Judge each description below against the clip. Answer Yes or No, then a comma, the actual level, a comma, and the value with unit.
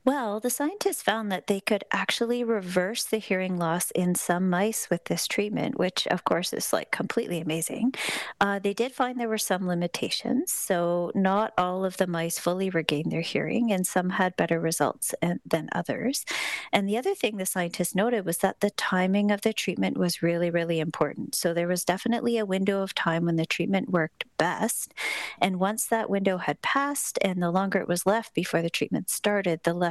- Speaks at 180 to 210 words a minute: Yes, average, 200 wpm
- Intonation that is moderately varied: Yes, average, 4.3 semitones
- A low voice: No, high, 190 Hz